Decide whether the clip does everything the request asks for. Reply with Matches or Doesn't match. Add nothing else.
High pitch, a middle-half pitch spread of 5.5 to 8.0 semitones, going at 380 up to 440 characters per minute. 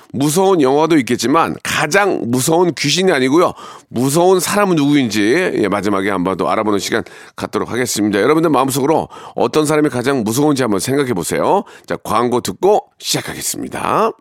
Doesn't match